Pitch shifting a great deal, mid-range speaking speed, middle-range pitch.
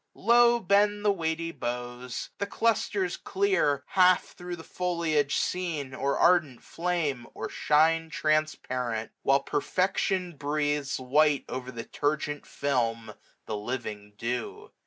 No: wide, 5.7 semitones; slow, 125 wpm; medium, 150 Hz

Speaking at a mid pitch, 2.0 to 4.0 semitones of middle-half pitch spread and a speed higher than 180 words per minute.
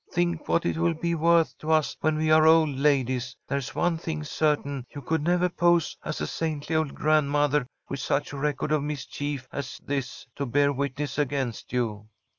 Yes: medium, 150 Hz; narrow, 2.4 semitones; average, 190 wpm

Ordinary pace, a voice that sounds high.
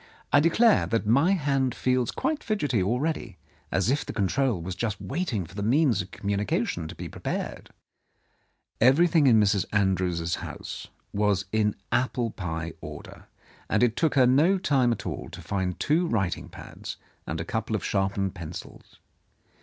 No: average, 160 wpm; low, 110 Hz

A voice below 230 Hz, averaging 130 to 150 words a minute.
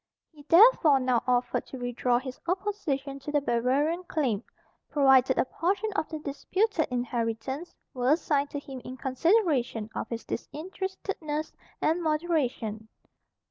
No: very high, 280 Hz; slow, 135 wpm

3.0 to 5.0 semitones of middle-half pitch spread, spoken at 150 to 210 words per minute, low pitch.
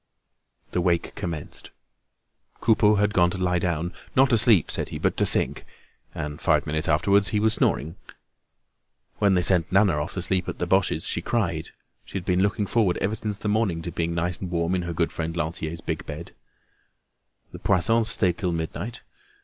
Yes: average, 3.3 semitones; average, 190 wpm; very low, 90 Hz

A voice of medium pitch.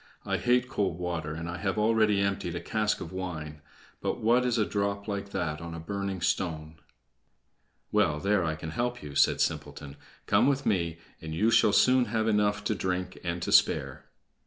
No: very low, 95 Hz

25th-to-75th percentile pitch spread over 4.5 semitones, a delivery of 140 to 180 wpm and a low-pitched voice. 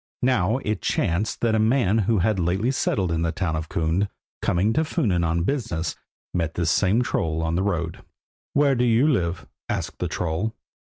No: average, 5.2 semitones; average, 190 wpm; very low, 95 Hz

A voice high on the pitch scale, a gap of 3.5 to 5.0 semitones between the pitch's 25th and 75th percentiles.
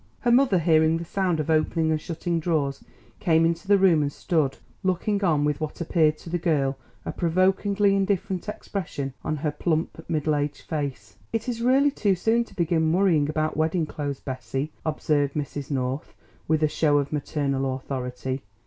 No: medium, 160 Hz; average, 4.0 semitones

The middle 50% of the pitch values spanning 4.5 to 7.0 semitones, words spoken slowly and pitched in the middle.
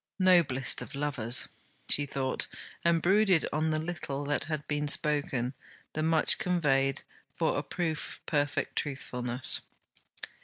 No: average, 3.0 semitones; slow, 130 wpm; medium, 145 Hz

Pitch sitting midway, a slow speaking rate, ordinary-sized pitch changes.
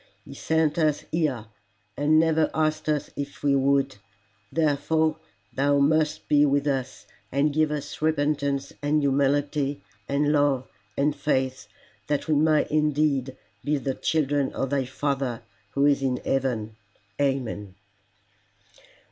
No: medium, 145 Hz; slow, 130 wpm; narrow, 1.9 semitones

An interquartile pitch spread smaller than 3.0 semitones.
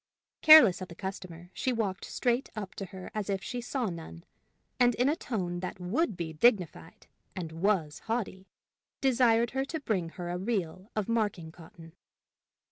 No: average, 5.1 semitones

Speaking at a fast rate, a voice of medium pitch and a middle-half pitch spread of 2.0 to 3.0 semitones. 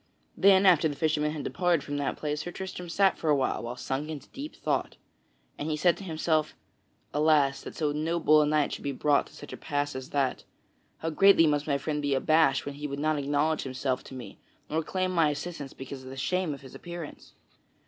Yes: fast, 220 wpm; medium, 150 Hz; narrow, 2.5 semitones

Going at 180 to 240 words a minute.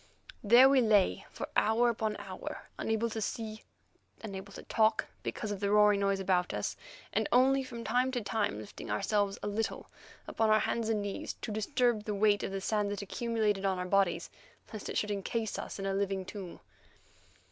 Yes: average, 190 wpm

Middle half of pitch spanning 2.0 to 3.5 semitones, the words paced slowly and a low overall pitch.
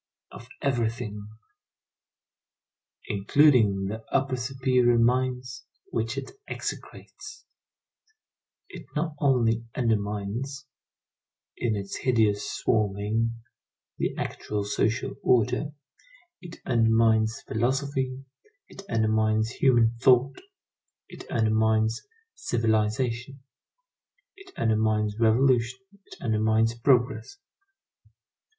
Yes: average, 2.8 semitones; slow, 80 wpm; low, 115 Hz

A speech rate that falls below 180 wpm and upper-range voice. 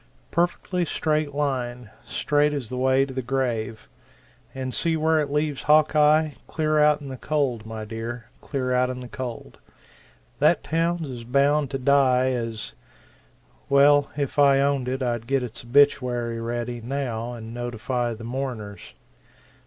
No: average, 155 wpm; low, 130 Hz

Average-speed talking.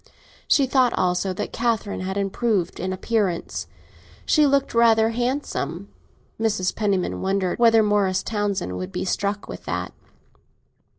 No: slow, 130 wpm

